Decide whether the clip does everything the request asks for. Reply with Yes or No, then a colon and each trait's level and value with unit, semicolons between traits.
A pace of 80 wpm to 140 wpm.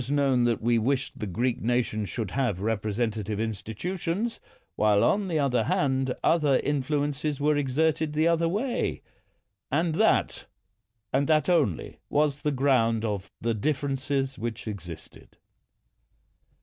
Yes: slow, 135 wpm